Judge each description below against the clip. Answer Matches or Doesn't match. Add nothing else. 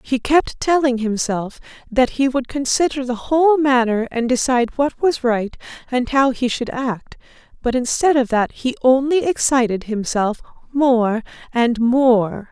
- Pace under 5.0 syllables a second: Matches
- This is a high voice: Matches